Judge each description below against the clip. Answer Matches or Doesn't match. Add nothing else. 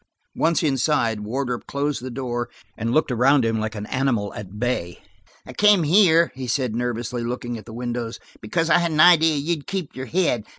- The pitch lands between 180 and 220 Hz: Doesn't match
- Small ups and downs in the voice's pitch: Doesn't match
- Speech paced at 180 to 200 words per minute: Matches